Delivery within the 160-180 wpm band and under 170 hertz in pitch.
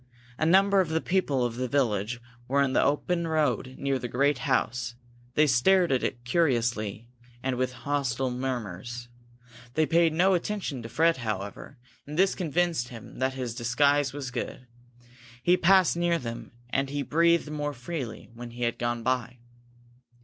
Yes: average, 165 wpm; low, 135 Hz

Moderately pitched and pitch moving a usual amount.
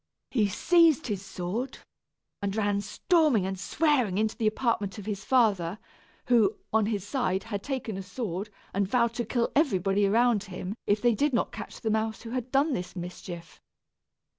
No: high, 215 Hz; average, 4.0 semitones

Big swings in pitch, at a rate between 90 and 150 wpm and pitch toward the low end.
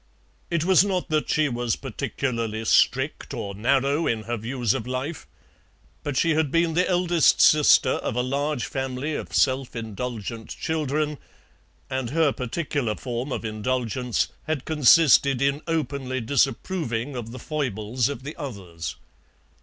No: average, 4.4 semitones; average, 145 wpm; low, 130 Hz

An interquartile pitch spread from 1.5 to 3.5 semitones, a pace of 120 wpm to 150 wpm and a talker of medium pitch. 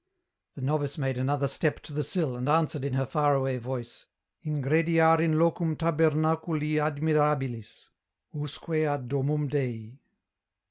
Yes: average, 2.8 semitones; average, 145 wpm; medium, 150 Hz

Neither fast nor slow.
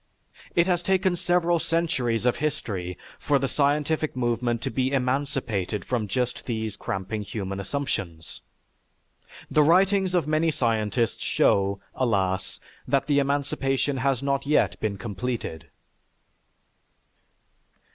No: slow, 115 wpm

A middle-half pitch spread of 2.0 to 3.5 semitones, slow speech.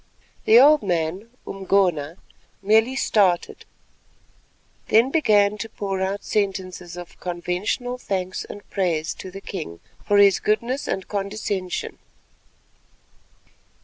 Yes: average, 2.9 semitones; slow, 110 wpm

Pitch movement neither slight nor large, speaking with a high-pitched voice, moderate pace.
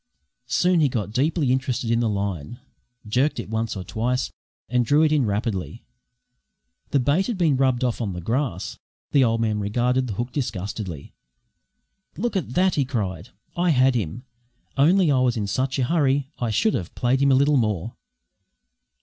No: average, 4.5 semitones; low, 125 Hz; average, 180 wpm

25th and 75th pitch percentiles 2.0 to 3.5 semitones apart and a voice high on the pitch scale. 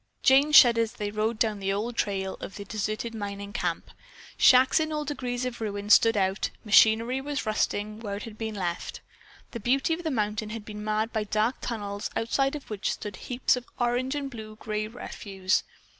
Yes: average, 2.9 semitones; high, 220 Hz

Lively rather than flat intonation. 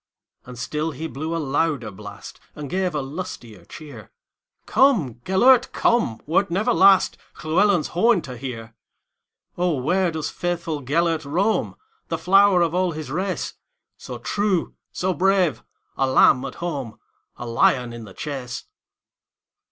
Yes: wide, 6.2 semitones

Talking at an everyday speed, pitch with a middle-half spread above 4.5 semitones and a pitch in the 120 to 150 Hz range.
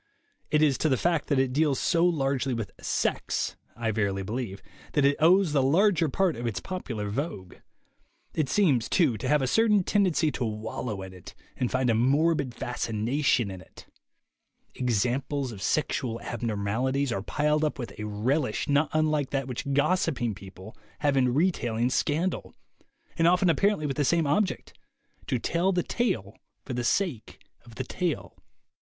Yes: average, 170 wpm; average, 5.3 semitones; low, 135 Hz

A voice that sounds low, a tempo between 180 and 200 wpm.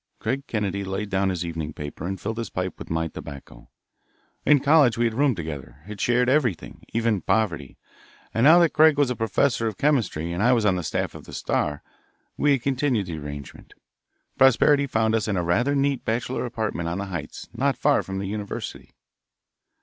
Yes: low, 110 Hz; average, 195 wpm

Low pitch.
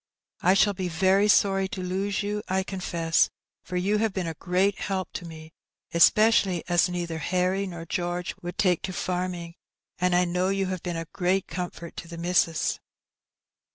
No: medium, 180 Hz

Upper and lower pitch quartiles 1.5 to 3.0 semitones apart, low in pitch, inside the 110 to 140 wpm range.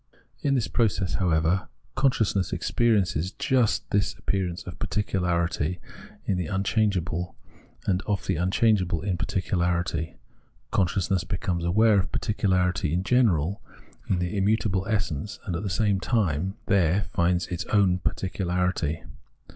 Yes: average, 2.7 semitones; very low, 95 Hz; slow, 135 wpm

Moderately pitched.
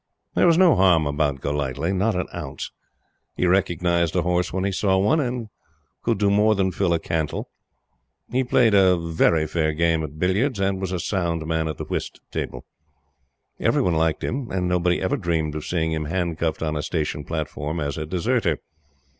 No: very low, 85 Hz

